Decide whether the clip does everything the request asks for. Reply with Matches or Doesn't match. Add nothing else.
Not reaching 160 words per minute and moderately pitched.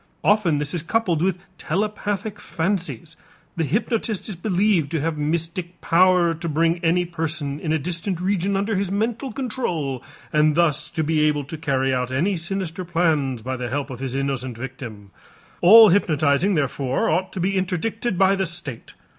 Doesn't match